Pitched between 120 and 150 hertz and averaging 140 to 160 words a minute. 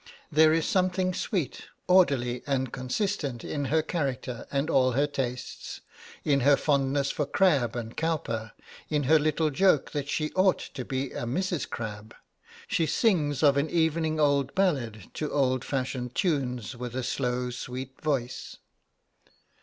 Yes: medium, 140 Hz; average, 150 wpm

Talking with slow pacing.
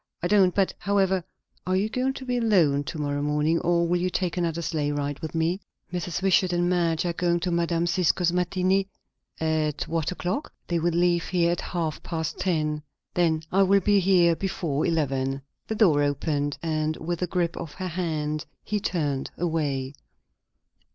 No: average, 180 wpm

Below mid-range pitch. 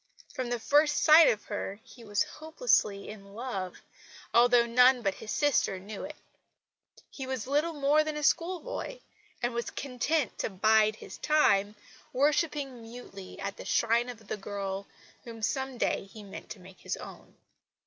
No: high, 240 Hz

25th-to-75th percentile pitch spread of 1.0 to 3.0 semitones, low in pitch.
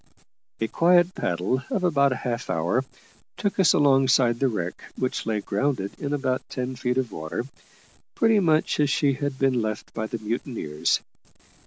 No: average, 4.4 semitones; low, 130 Hz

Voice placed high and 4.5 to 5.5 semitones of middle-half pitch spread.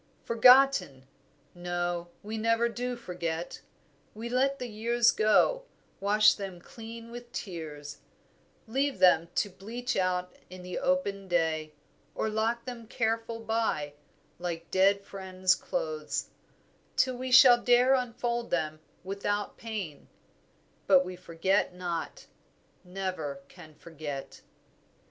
Yes: high, 205 Hz; average, 5.1 semitones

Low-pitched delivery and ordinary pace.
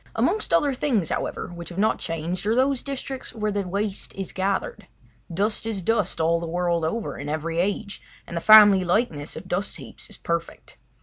No: high, 195 Hz; average, 190 wpm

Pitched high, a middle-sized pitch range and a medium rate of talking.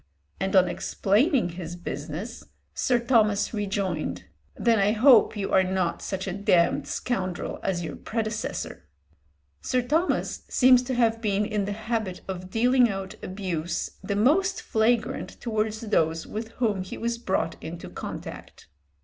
Yes: high, 210 Hz; average, 3.9 semitones; average, 145 wpm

